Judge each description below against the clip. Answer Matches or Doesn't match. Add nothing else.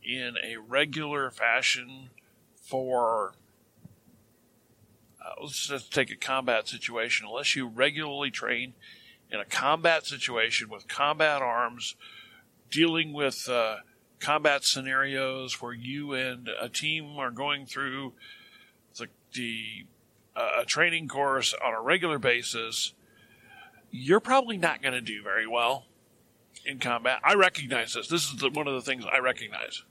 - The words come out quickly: Doesn't match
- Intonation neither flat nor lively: Matches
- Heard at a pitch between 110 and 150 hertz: Matches